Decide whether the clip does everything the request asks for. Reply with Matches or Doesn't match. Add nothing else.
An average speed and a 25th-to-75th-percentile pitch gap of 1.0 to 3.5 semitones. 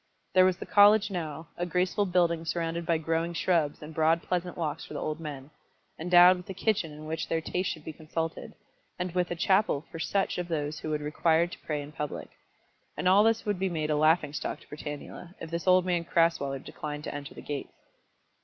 Doesn't match